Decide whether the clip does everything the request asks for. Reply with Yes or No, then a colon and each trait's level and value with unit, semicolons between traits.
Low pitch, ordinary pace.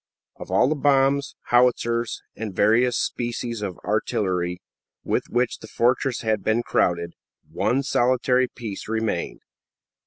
No: low, 120 Hz; slow, 125 wpm